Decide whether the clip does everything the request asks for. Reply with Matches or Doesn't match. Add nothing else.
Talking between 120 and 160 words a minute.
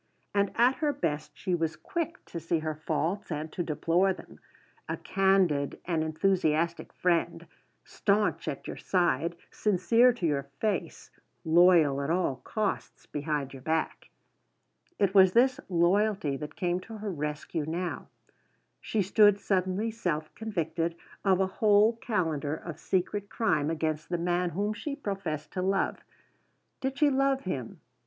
Matches